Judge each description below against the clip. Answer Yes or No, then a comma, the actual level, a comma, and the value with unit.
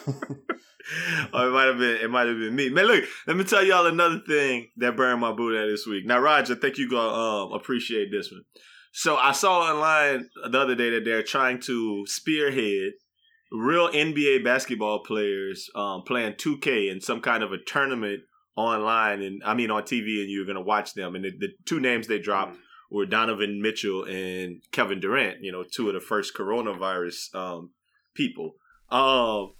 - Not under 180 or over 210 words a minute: Yes, average, 190 wpm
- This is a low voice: Yes, low, 115 Hz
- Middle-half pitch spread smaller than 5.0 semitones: No, wide, 5.4 semitones